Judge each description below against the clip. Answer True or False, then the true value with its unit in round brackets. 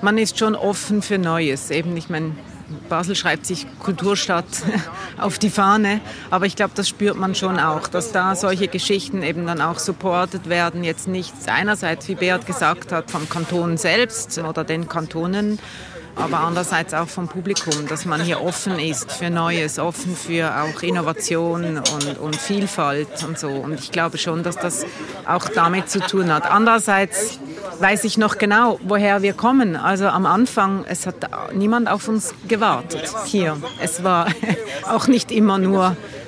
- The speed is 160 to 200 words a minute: True (170 wpm)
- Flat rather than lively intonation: False (3.6 semitones)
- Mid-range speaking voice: True (180 Hz)